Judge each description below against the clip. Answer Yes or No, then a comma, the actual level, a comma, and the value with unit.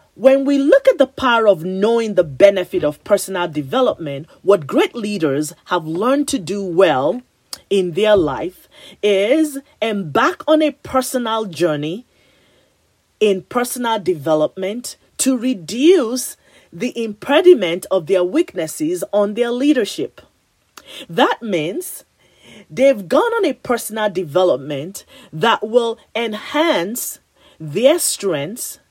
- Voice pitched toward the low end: No, high, 220 Hz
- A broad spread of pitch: Yes, wide, 6.5 semitones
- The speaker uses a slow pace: Yes, slow, 115 wpm